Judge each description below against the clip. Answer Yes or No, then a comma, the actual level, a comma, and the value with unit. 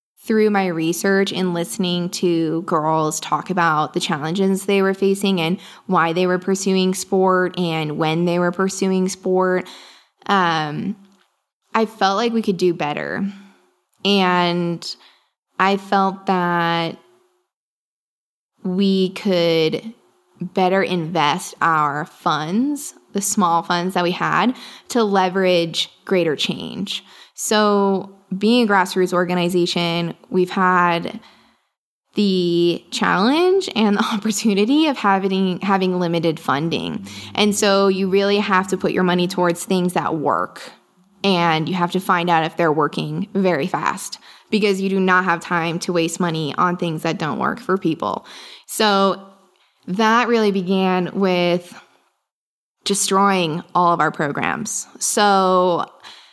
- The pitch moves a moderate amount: No, narrow, 2.3 semitones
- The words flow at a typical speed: No, slow, 130 wpm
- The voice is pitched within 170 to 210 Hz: Yes, medium, 185 Hz